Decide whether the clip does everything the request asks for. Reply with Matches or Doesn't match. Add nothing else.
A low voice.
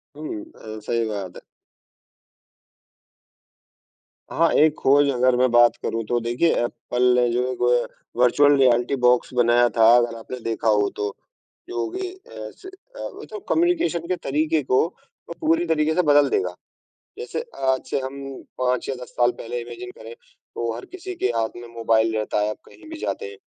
Matches